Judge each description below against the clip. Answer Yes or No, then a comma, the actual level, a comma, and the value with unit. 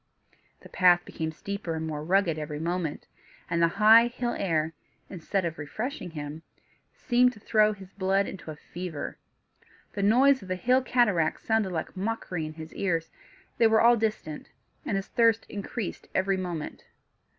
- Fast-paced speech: No, average, 165 wpm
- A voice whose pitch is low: No, high, 190 Hz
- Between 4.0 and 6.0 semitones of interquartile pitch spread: Yes, average, 5.2 semitones